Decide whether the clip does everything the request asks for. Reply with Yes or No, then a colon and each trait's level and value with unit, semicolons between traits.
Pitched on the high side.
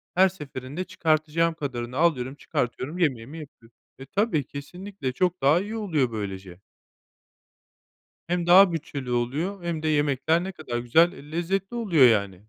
No: medium, 155 Hz